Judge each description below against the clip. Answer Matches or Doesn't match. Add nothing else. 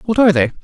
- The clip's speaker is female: Matches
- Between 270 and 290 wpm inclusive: Matches